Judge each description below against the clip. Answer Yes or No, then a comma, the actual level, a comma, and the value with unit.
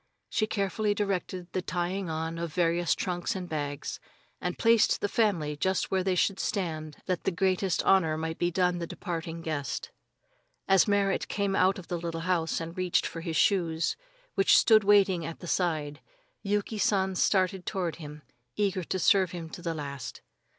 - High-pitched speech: No, medium, 180 Hz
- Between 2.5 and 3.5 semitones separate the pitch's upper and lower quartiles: Yes, average, 2.9 semitones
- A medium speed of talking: Yes, average, 180 wpm